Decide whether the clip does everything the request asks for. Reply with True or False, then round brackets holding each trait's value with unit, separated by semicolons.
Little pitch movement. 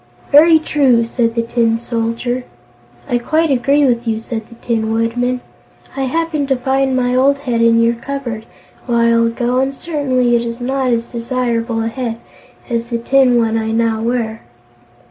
True (2.3 semitones)